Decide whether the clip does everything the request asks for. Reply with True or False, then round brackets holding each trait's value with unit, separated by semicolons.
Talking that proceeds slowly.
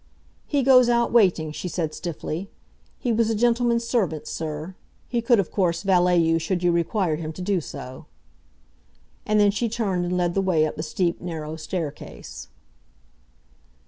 False (170 wpm)